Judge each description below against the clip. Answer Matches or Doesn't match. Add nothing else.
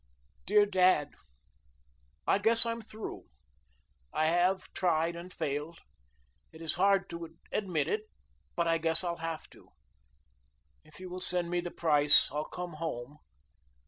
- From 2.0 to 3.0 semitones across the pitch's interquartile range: Matches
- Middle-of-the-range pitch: Matches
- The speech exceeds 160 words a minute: Doesn't match